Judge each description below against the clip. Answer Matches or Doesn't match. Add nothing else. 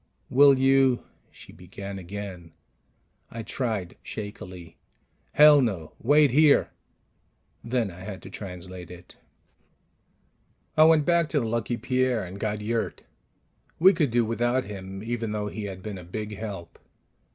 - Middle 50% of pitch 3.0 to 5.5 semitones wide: Matches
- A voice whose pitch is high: Doesn't match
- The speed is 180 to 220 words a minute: Doesn't match